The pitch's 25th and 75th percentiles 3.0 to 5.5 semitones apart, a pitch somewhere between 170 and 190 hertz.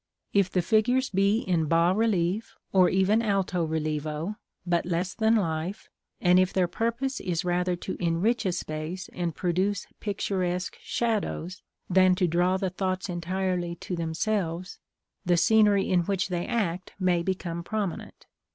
No: narrow, 2.6 semitones; medium, 185 Hz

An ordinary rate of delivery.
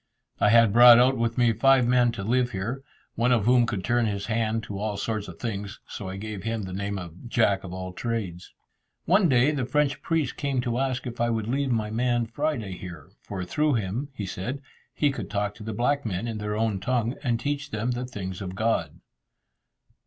No: fast, 220 wpm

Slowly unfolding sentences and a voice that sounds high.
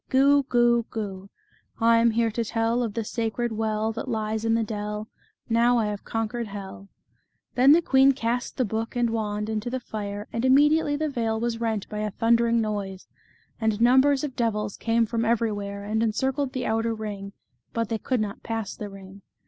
No: average, 195 wpm; high, 225 Hz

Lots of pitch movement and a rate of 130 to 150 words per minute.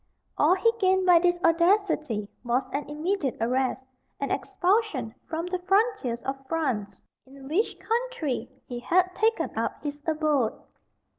Yes: wide, 5.9 semitones; average, 140 wpm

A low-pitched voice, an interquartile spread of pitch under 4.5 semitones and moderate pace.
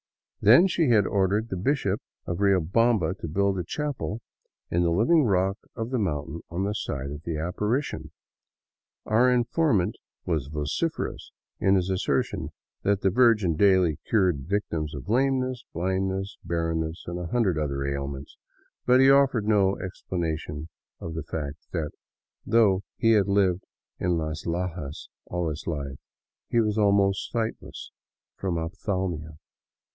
No: very low, 95 Hz; average, 4.9 semitones; average, 150 wpm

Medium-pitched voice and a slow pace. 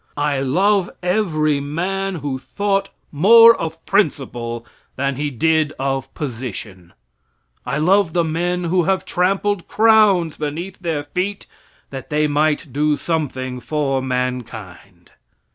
Yes: medium, 155 Hz; slow, 125 wpm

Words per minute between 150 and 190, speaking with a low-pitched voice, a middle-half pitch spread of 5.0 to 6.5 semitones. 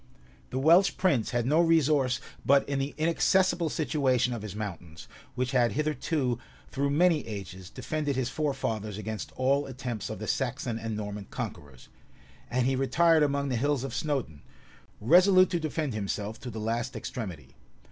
Yes: average, 160 wpm; low, 130 Hz; wide, 5.4 semitones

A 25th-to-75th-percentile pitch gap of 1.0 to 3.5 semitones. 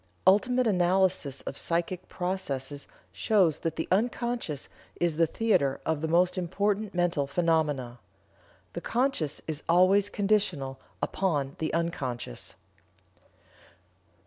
No: average, 4.8 semitones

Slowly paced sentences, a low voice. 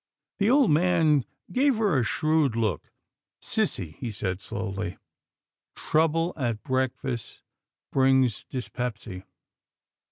Yes: slow, 120 wpm; low, 130 Hz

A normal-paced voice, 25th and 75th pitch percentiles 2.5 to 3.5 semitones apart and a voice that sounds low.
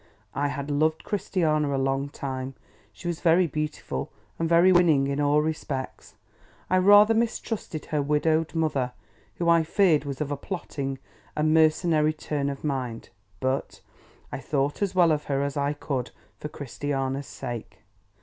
No: average, 160 wpm; average, 2.9 semitones; medium, 150 Hz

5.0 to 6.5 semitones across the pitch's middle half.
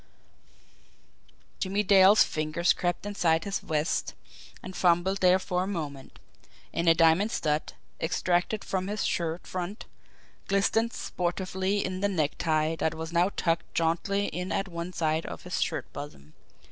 No: average, 3.0 semitones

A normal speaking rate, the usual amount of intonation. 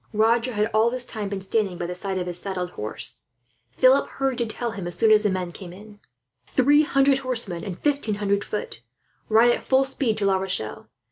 No: fast, 210 wpm; average, 4.4 semitones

